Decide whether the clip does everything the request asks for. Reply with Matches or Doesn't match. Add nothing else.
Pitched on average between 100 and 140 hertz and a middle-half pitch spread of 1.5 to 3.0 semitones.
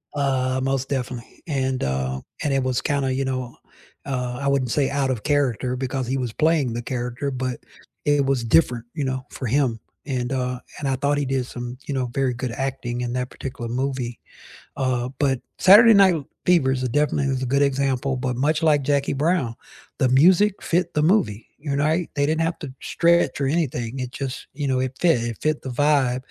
Matches